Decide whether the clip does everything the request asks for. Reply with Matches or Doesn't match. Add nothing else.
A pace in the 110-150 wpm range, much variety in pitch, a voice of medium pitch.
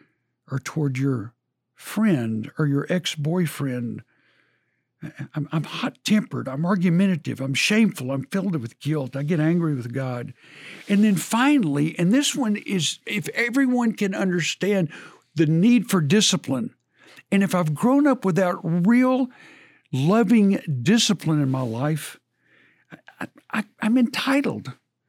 Matches